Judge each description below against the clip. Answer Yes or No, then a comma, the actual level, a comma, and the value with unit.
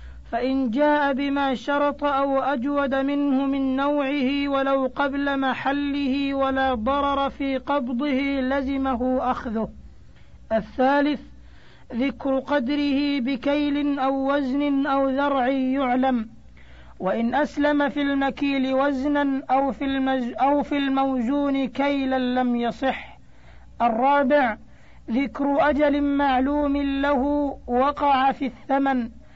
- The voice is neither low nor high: No, very high, 275 Hz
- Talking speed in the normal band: Yes, average, 95 wpm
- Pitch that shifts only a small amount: Yes, narrow, 1.5 semitones